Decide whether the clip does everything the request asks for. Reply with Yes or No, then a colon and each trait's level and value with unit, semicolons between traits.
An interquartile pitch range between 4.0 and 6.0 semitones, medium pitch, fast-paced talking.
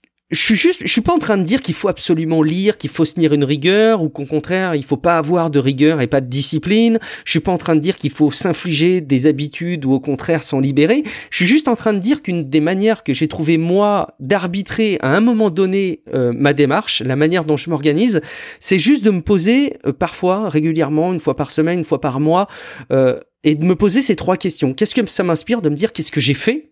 Yes: average, 5.1 semitones; medium, 170 Hz; fast, 250 wpm